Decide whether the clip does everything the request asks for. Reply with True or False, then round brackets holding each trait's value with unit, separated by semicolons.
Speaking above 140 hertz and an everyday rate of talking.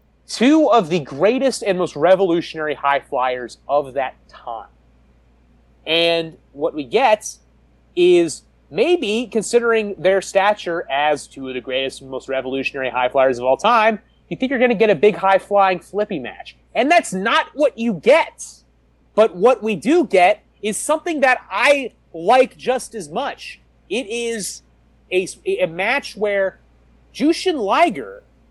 True (190 Hz; 155 wpm)